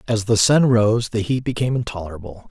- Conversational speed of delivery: Yes, average, 190 wpm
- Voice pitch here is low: Yes, low, 110 Hz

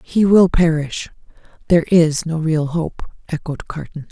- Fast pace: No, average, 145 wpm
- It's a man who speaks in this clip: No, female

